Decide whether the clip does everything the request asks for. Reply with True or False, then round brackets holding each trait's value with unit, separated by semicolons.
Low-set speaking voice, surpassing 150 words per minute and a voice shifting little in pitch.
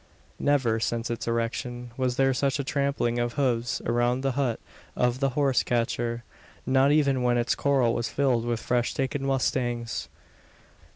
True (125 Hz; 160 wpm; 2.3 semitones)